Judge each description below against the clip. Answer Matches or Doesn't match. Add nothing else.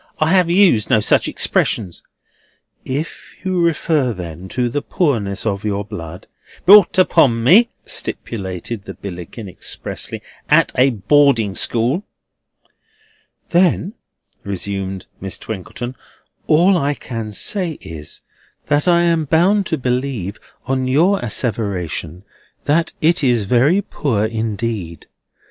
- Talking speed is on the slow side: Matches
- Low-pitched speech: Matches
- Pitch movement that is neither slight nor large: Doesn't match